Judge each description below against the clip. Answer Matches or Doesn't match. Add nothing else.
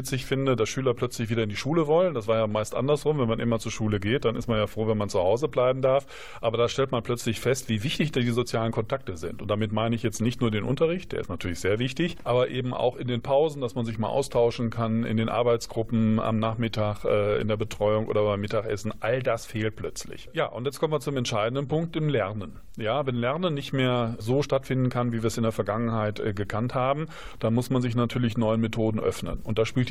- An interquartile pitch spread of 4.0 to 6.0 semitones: Doesn't match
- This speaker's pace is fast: Matches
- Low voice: Matches